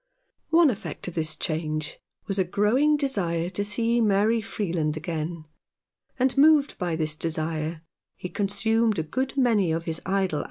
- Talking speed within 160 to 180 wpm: Yes, average, 170 wpm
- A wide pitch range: Yes, wide, 5.9 semitones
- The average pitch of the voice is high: Yes, high, 195 Hz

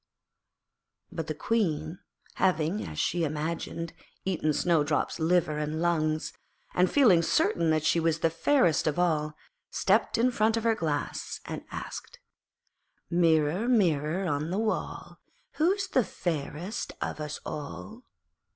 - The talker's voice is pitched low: No, medium, 165 Hz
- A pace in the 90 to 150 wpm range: Yes, slow, 135 wpm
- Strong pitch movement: No, average, 4.1 semitones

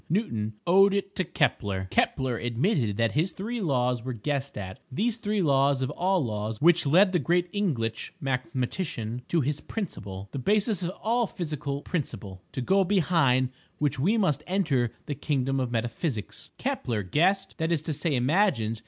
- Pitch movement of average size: No, wide, 7.1 semitones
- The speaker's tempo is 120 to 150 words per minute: No, average, 160 wpm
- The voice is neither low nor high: Yes, medium, 145 Hz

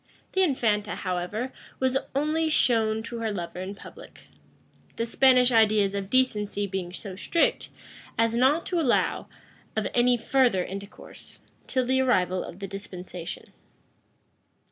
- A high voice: Yes, high, 220 Hz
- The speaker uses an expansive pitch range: No, average, 4.7 semitones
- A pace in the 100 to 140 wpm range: Yes, slow, 135 wpm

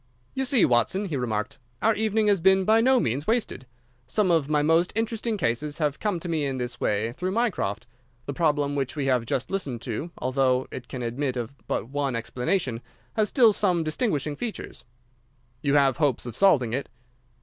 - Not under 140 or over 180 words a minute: No, average, 190 wpm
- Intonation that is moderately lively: No, wide, 7.4 semitones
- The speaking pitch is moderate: Yes, medium, 145 Hz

